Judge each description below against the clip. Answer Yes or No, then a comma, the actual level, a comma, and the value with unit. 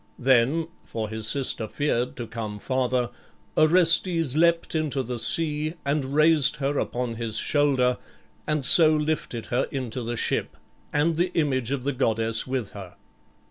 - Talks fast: No, average, 150 wpm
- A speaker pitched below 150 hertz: Yes, low, 135 Hz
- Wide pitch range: No, average, 4.3 semitones